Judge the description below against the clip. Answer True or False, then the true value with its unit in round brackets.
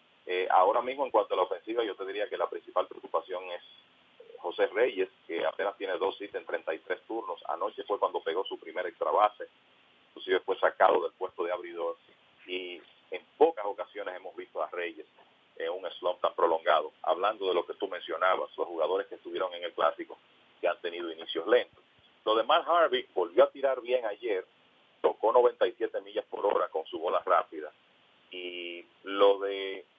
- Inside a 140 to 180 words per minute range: False (190 wpm)